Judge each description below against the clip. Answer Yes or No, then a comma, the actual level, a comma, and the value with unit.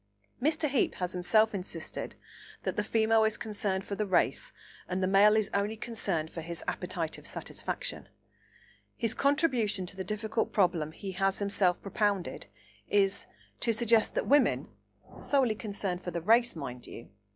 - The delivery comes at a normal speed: Yes, average, 155 wpm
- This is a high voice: Yes, high, 205 Hz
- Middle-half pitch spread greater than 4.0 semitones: No, average, 3.7 semitones